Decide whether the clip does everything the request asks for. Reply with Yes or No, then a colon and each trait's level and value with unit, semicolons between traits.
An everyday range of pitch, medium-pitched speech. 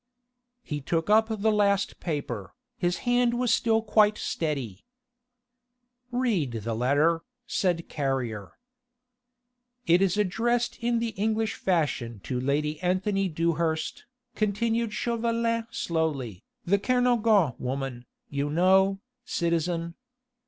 No: wide, 7.0 semitones; medium, 180 Hz